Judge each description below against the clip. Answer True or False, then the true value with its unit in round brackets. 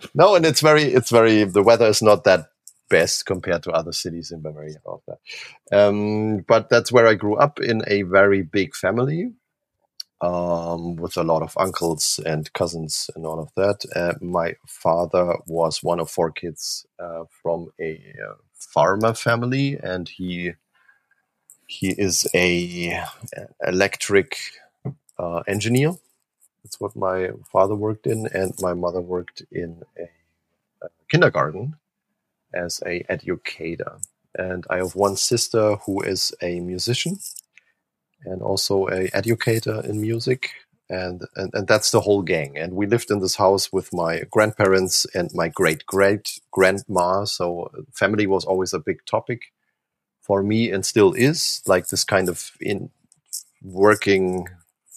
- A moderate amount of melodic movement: True (4.1 semitones)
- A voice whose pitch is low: True (95 Hz)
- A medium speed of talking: True (145 wpm)